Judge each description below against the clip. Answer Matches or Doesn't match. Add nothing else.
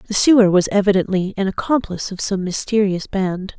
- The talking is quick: Doesn't match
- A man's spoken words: Doesn't match